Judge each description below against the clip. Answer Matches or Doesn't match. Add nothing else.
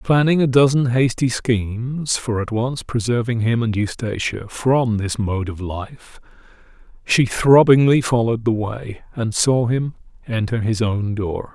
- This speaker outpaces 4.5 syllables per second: Doesn't match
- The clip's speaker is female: Doesn't match